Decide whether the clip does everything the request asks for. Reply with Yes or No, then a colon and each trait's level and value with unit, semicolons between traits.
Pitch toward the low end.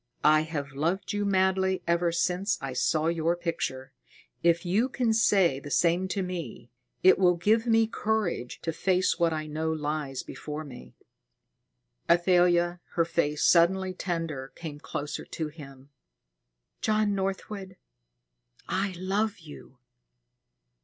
No: medium, 170 Hz